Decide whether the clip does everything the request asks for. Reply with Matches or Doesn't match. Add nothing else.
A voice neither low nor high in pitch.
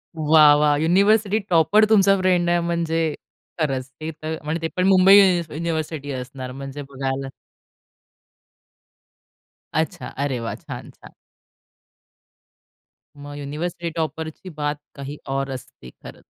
Matches